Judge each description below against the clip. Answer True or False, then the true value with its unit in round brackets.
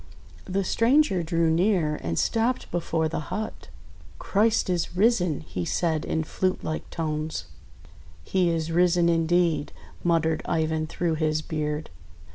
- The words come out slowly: True (130 wpm)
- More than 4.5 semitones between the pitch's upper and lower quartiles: False (2.5 semitones)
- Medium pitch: True (165 Hz)